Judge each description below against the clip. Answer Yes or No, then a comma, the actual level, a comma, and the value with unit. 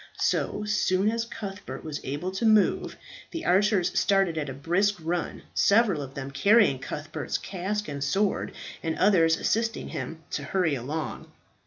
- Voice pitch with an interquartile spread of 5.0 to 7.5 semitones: Yes, wide, 5.5 semitones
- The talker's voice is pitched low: No, medium, 185 Hz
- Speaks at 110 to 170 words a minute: Yes, average, 155 wpm